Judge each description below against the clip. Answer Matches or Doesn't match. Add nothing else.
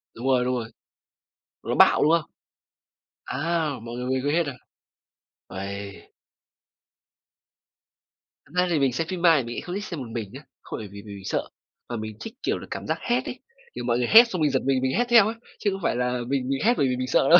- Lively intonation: Matches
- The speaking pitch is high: Doesn't match